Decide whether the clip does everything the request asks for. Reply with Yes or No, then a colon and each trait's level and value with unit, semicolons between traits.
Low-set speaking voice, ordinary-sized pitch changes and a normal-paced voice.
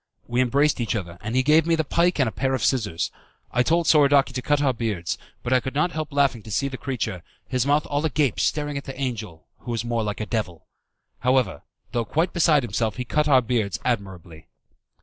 No: low, 130 Hz; average, 4.5 semitones; fast, 225 wpm